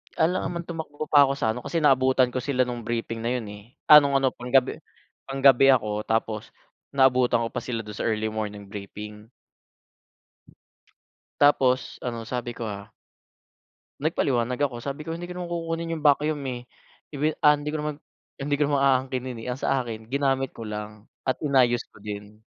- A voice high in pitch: No, low, 130 Hz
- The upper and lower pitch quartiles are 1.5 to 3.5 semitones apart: No, average, 4.0 semitones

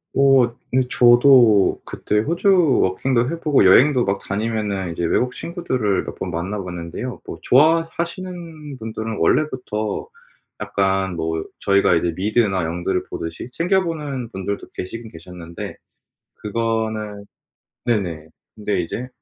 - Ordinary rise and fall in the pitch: No, wide, 6.0 semitones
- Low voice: Yes, low, 110 Hz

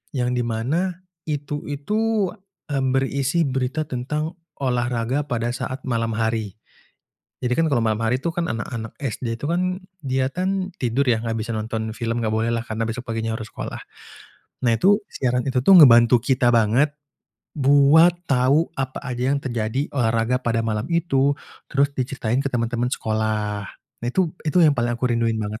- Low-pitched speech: Yes, low, 125 Hz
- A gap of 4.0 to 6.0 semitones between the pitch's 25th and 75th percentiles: No, average, 3.6 semitones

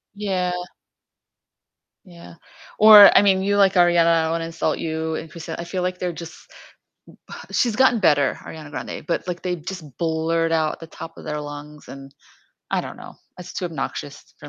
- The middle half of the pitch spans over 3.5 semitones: No, narrow, 2.5 semitones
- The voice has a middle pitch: Yes, medium, 165 Hz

